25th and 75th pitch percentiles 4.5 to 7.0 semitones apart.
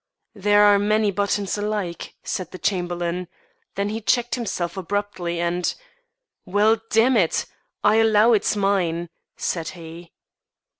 No: average, 3.3 semitones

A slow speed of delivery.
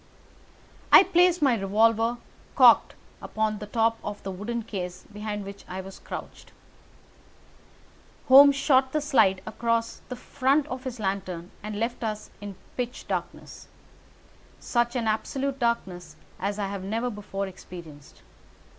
Yes: slow, 130 wpm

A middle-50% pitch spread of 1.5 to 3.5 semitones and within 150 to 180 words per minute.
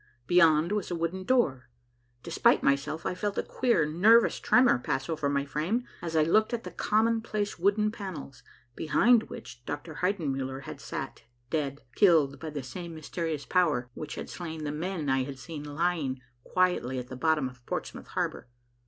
No: average, 5.1 semitones; average, 170 wpm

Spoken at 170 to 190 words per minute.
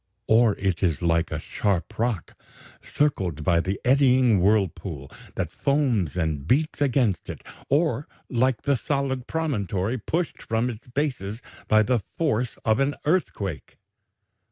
No: slow, 135 wpm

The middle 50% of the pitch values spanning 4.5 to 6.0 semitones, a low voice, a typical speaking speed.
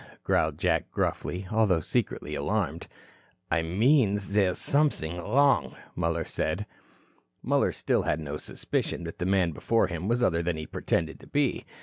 Yes: average, 4.9 semitones; very low, 90 Hz; average, 150 wpm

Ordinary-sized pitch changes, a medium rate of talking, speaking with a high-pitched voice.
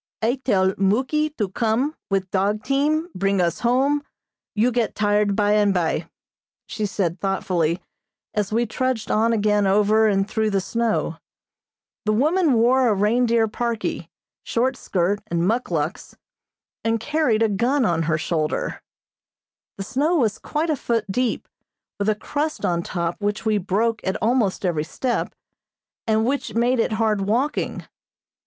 Yes: average, 3.8 semitones; average, 150 wpm; high, 215 Hz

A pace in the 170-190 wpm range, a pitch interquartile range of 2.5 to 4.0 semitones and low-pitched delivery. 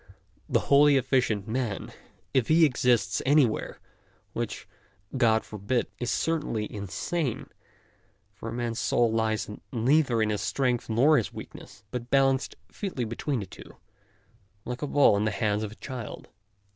No: average, 155 wpm; average, 3.7 semitones; low, 120 Hz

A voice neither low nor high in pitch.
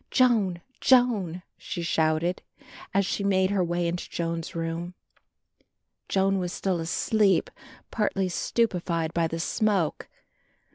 Yes: medium, 180 Hz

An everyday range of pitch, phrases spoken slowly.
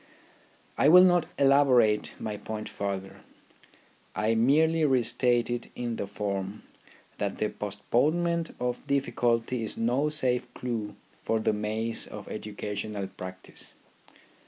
Yes: average, 4.5 semitones; slow, 120 wpm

